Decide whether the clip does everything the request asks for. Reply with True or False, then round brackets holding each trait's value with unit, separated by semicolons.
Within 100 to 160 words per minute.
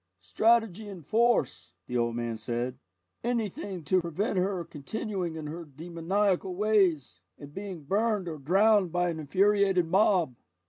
True (140 wpm)